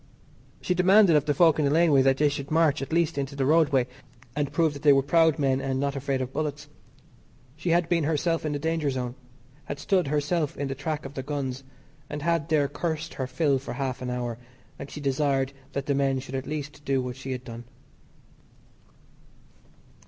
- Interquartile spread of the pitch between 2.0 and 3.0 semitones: Yes, narrow, 2.6 semitones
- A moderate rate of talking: No, fast, 210 wpm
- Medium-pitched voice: Yes, medium, 145 Hz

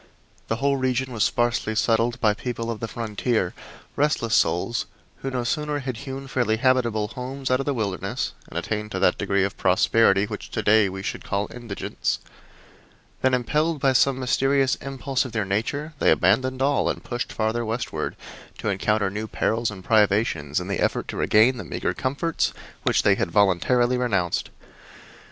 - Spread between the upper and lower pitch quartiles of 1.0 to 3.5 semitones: No, average, 3.9 semitones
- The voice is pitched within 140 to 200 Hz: No, low, 115 Hz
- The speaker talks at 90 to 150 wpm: No, average, 175 wpm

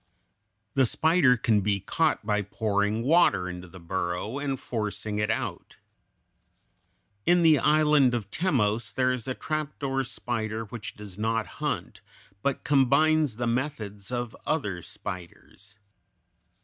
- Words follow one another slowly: Yes, slow, 130 wpm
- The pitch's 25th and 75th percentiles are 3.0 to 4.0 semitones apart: No, average, 5.1 semitones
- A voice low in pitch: Yes, low, 115 Hz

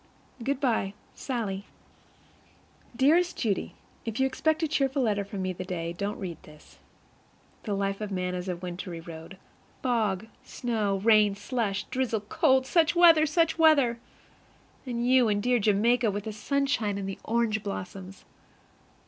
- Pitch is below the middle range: No, high, 215 Hz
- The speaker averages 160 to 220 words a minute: No, average, 150 wpm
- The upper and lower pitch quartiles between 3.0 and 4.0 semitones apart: No, average, 5.1 semitones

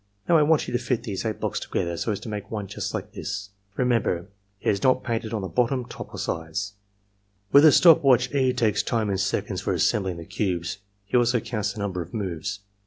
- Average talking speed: No, fast, 240 wpm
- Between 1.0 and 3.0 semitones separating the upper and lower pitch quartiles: No, average, 4.1 semitones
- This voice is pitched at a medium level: No, low, 105 Hz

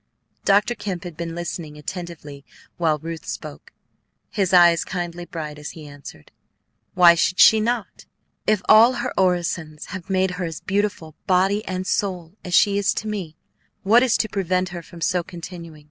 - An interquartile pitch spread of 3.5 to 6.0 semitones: No, average, 2.9 semitones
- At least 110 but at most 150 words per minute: No, average, 170 wpm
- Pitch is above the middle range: No, medium, 180 Hz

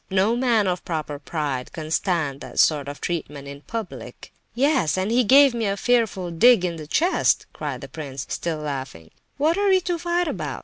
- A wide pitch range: Yes, wide, 8.5 semitones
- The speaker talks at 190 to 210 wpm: Yes, average, 195 wpm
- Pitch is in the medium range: Yes, medium, 180 Hz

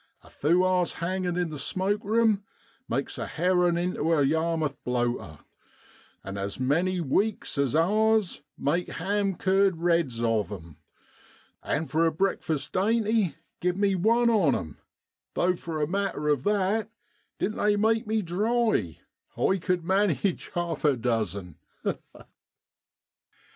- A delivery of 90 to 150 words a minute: Yes, average, 140 wpm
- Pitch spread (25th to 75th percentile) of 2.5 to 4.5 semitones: No, average, 5.3 semitones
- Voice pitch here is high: No, medium, 175 Hz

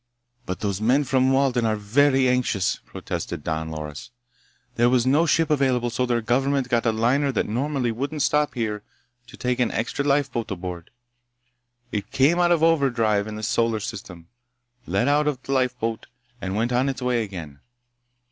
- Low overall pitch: Yes, low, 120 Hz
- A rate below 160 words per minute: No, average, 170 wpm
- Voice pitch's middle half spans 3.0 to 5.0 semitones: Yes, average, 4.1 semitones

